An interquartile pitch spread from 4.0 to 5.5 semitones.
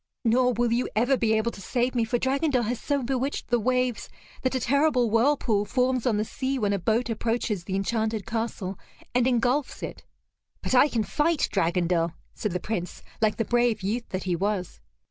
No: average, 3.2 semitones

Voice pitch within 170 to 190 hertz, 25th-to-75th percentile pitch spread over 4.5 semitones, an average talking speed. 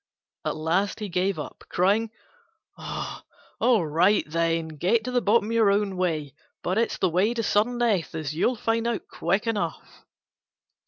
No: high, 200 Hz; average, 5.2 semitones; average, 160 wpm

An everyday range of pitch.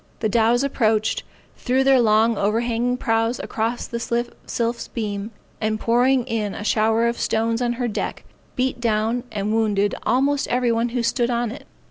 No: narrow, 1.8 semitones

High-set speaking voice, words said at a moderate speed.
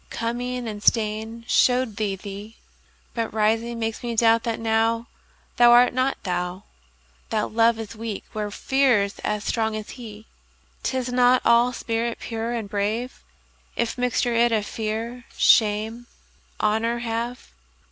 No: high, 225 Hz; slow, 125 wpm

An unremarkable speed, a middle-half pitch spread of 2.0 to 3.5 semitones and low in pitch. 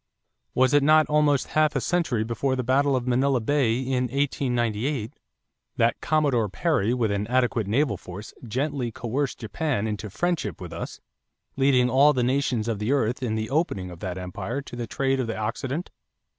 No: average, 180 wpm; average, 4.1 semitones; low, 125 Hz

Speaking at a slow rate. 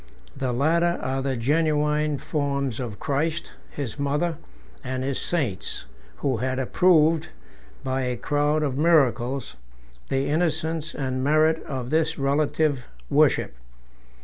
Yes: slow, 120 wpm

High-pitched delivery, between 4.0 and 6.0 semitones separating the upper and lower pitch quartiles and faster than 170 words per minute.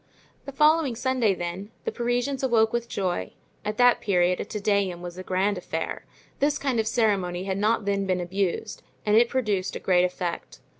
Yes: high, 205 Hz; average, 4.6 semitones; average, 190 wpm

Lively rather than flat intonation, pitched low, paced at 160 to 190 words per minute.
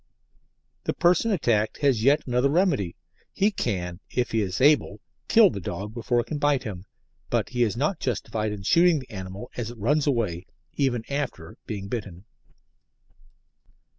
Yes: wide, 6.1 semitones; low, 120 Hz; average, 165 wpm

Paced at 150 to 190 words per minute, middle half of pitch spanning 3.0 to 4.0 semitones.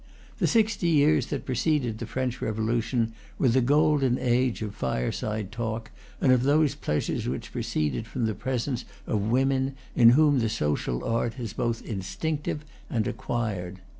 Yes: average, 155 wpm; average, 3.6 semitones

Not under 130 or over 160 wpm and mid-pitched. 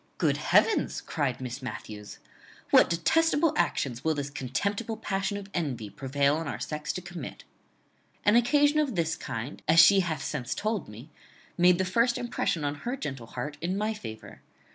No: average, 170 wpm; medium, 165 Hz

